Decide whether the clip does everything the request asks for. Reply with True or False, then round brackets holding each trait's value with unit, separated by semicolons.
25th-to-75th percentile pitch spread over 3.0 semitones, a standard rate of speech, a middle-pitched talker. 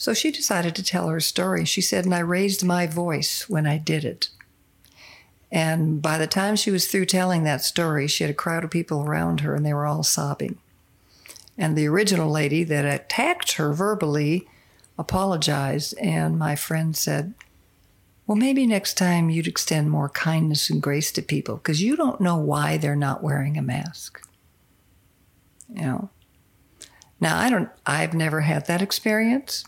True (3.8 semitones; 175 wpm; 160 Hz)